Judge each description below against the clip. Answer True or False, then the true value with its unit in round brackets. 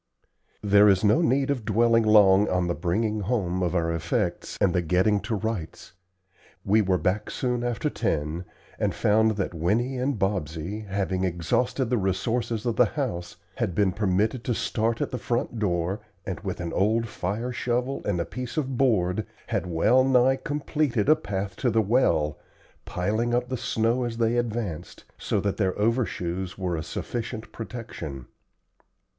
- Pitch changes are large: False (4.6 semitones)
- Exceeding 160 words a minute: True (170 wpm)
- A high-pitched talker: False (105 Hz)